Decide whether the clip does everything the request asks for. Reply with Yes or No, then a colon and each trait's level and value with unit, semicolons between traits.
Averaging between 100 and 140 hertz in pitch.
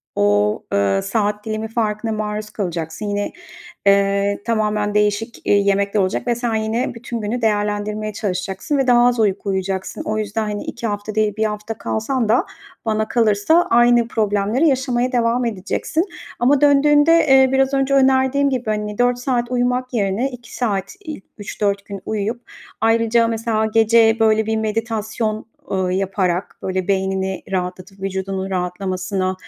No: high, 215 Hz